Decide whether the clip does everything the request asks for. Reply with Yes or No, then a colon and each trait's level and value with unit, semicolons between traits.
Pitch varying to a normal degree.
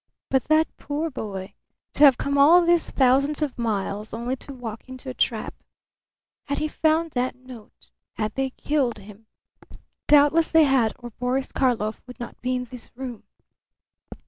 Yes: average, 3.7 semitones